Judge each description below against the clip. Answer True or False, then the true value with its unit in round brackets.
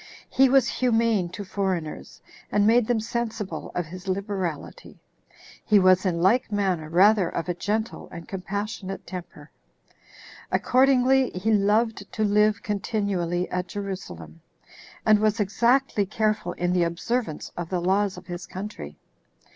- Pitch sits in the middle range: False (200 Hz)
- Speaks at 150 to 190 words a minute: False (140 wpm)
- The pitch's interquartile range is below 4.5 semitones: True (3.4 semitones)